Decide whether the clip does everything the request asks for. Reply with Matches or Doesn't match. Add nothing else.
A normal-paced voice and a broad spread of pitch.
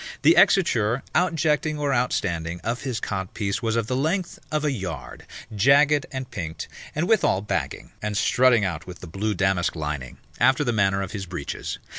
Matches